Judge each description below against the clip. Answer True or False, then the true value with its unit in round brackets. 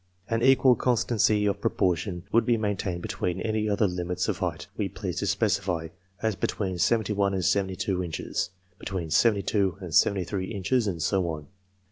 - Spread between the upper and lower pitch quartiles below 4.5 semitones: True (3.1 semitones)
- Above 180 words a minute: True (190 wpm)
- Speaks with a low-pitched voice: True (100 Hz)